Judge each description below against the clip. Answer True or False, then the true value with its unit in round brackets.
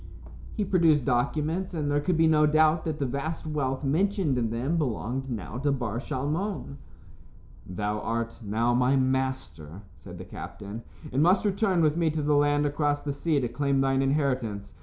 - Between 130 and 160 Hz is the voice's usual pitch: True (140 Hz)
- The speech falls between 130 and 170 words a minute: False (180 wpm)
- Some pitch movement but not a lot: True (4.2 semitones)